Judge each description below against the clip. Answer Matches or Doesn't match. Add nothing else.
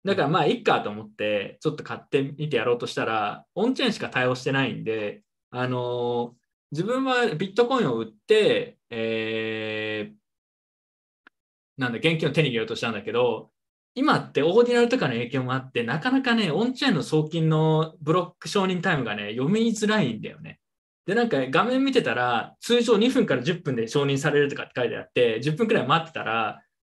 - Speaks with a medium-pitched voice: Matches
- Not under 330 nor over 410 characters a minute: Matches